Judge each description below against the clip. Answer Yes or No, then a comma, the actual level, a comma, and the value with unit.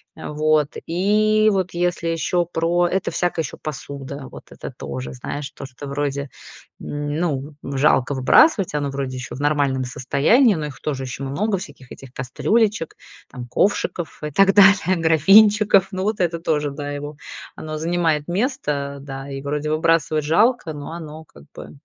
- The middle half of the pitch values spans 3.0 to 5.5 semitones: Yes, average, 4.2 semitones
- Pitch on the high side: No, medium, 155 Hz